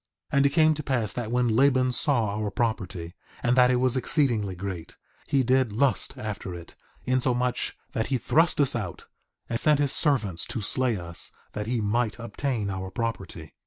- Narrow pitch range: No, average, 4.1 semitones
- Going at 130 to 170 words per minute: No, average, 185 wpm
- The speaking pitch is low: Yes, low, 120 Hz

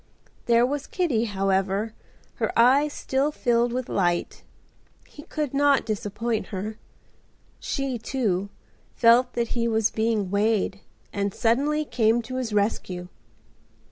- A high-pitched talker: Yes, high, 230 Hz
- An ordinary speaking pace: No, slow, 125 wpm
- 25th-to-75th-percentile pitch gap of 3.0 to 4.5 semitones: Yes, average, 4.0 semitones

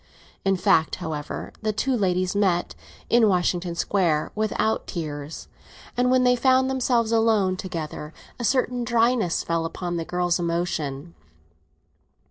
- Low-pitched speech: No, medium, 185 Hz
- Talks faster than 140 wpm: No, slow, 135 wpm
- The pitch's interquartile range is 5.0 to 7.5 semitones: Yes, wide, 5.5 semitones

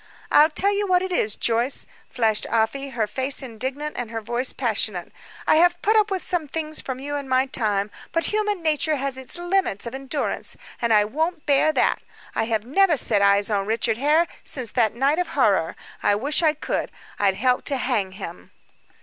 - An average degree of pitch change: No, wide, 5.8 semitones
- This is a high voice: Yes, very high, 265 Hz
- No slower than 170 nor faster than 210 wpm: Yes, average, 200 wpm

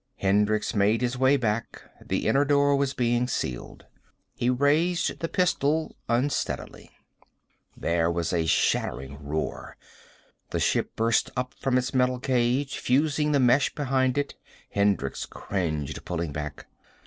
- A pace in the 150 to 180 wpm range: No, slow, 135 wpm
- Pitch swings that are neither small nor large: No, wide, 6.0 semitones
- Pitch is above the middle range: No, low, 125 Hz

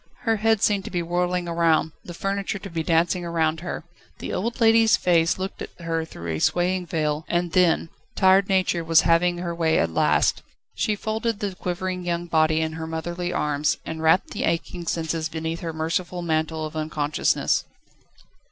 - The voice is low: No, medium, 170 Hz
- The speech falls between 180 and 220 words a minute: Yes, average, 190 wpm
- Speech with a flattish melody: Yes, narrow, 2.3 semitones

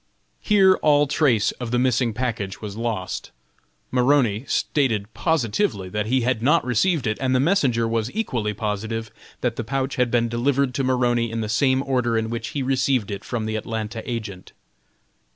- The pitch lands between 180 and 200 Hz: No, low, 120 Hz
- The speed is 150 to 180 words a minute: Yes, average, 175 wpm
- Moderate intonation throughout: Yes, average, 3.2 semitones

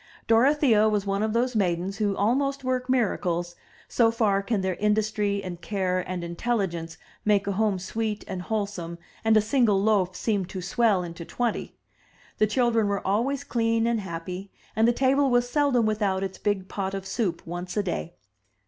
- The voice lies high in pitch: Yes, high, 205 Hz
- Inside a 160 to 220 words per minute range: Yes, average, 175 wpm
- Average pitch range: Yes, average, 3.4 semitones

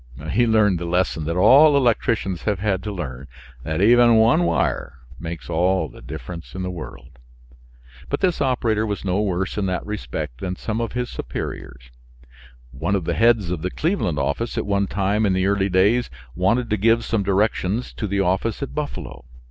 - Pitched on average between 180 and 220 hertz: No, low, 100 Hz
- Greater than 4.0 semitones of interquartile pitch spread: Yes, average, 4.5 semitones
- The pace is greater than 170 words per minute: Yes, average, 190 wpm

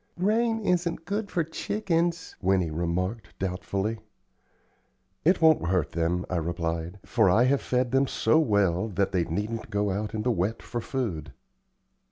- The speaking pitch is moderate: No, low, 105 Hz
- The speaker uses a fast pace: No, average, 155 wpm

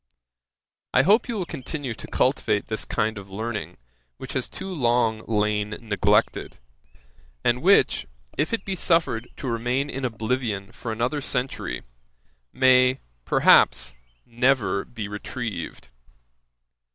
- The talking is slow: Yes, slow, 125 wpm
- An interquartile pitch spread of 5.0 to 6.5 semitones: No, average, 4.0 semitones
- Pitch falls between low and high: No, low, 120 Hz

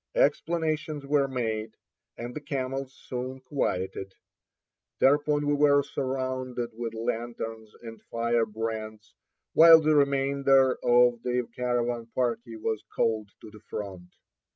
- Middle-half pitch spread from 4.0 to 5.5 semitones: No, average, 3.5 semitones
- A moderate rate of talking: No, slow, 115 wpm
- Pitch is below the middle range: Yes, low, 125 Hz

